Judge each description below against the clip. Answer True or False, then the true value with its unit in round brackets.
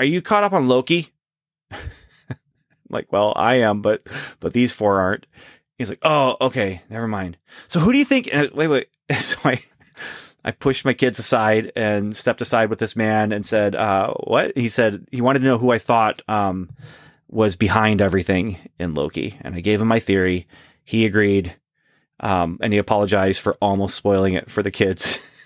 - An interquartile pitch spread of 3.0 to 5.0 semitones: True (4.1 semitones)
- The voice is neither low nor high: False (110 Hz)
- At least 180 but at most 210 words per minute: True (190 wpm)